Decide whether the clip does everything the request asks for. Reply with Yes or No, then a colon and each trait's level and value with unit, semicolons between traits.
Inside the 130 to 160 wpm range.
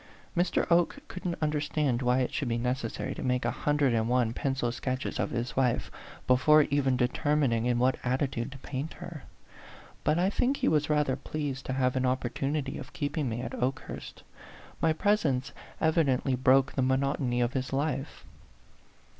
No: average, 175 wpm